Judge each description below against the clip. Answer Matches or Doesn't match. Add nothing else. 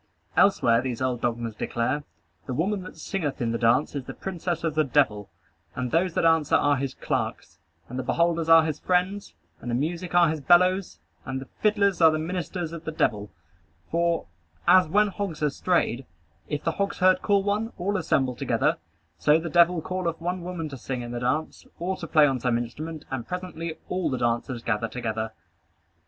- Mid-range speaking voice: Matches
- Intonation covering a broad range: Matches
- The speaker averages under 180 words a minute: Doesn't match